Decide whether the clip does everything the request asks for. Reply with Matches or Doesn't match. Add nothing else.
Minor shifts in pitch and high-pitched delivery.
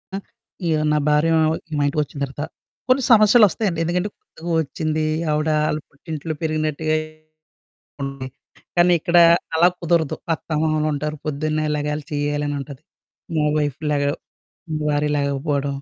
Doesn't match